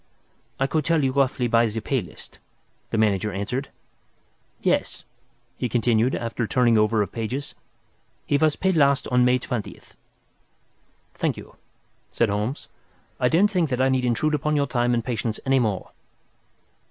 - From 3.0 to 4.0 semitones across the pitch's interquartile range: Yes, average, 3.6 semitones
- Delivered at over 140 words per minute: Yes, average, 165 wpm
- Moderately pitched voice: No, low, 125 Hz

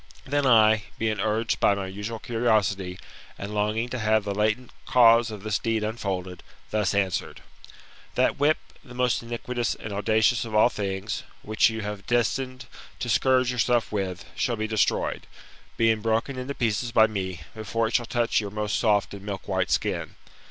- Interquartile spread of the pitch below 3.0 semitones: Yes, narrow, 2.5 semitones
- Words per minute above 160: Yes, average, 175 wpm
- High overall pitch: No, low, 110 Hz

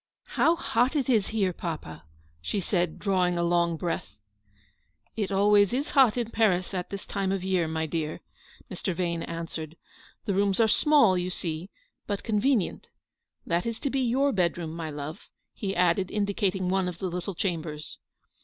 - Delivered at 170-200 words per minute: Yes, average, 180 wpm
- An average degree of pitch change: Yes, average, 3.6 semitones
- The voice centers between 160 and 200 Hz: Yes, medium, 185 Hz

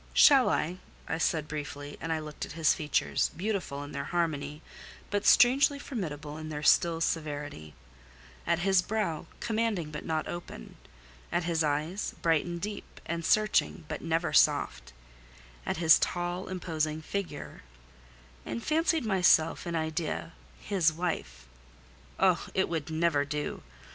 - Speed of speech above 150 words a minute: No, average, 145 wpm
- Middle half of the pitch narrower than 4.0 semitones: Yes, average, 3.3 semitones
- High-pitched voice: No, medium, 165 Hz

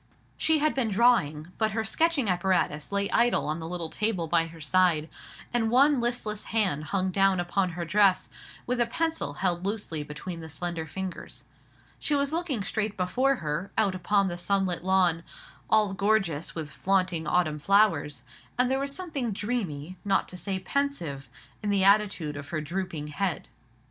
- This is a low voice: No, high, 190 Hz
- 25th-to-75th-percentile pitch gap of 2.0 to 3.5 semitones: No, average, 4.8 semitones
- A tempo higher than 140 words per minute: Yes, average, 170 wpm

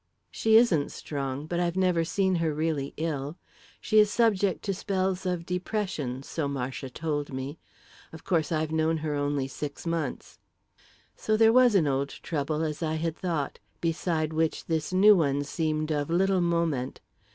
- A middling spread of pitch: Yes, average, 3.8 semitones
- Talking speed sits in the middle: Yes, average, 165 wpm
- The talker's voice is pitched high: No, medium, 160 Hz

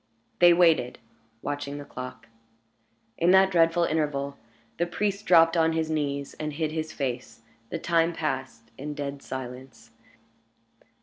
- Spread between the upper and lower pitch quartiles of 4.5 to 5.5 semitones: No, average, 3.4 semitones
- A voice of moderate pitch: Yes, medium, 150 Hz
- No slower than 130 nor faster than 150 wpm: Yes, slow, 135 wpm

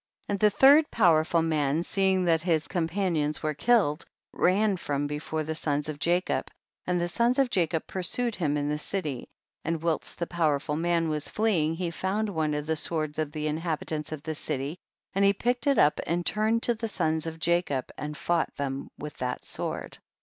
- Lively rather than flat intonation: No, average, 3.9 semitones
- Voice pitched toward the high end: No, medium, 165 Hz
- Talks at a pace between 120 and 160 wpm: No, average, 195 wpm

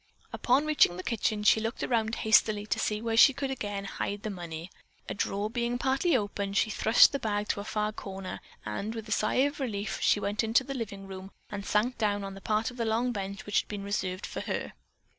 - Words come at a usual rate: No, fast, 230 wpm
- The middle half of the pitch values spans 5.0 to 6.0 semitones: No, average, 2.7 semitones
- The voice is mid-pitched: No, high, 215 Hz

